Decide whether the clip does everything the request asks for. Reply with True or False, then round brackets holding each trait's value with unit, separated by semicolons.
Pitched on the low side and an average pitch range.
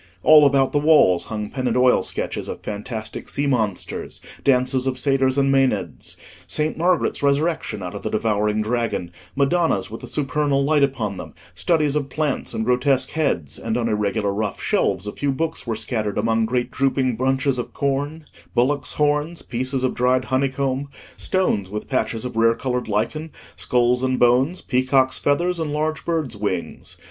True (130 Hz; 4.1 semitones)